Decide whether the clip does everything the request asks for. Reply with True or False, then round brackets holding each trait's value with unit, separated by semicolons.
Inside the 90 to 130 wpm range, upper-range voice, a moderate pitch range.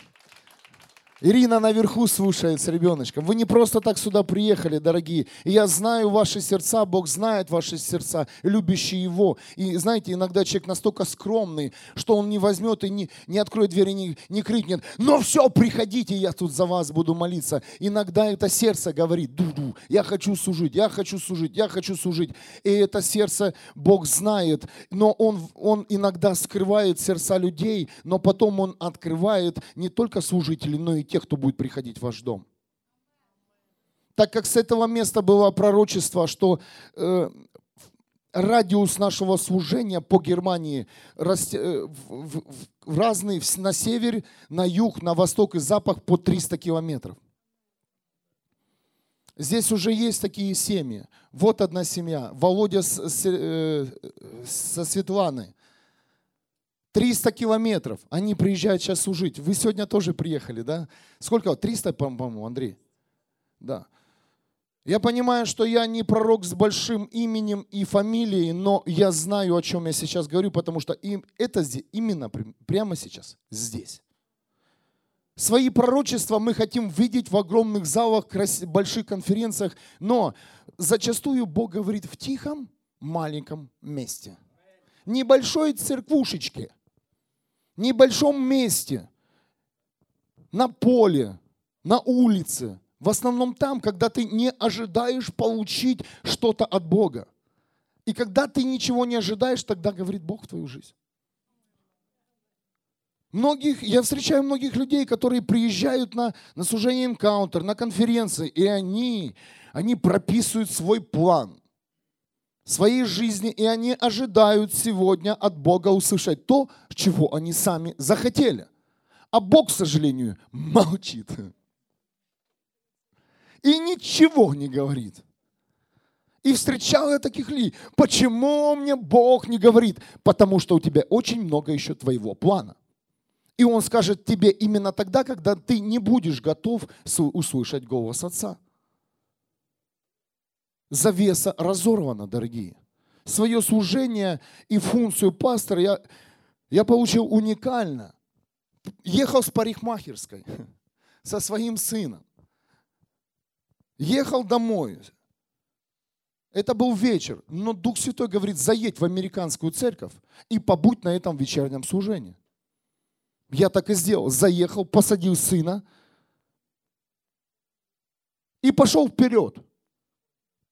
True (125 wpm; 200 Hz; 4.9 semitones)